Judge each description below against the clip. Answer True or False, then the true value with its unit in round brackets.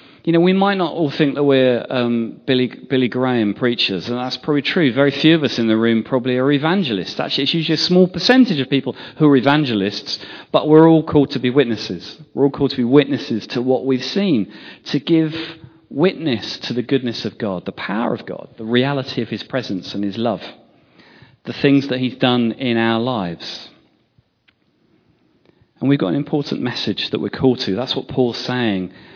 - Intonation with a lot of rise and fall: False (3.7 semitones)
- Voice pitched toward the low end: True (130 Hz)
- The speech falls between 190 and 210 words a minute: True (200 wpm)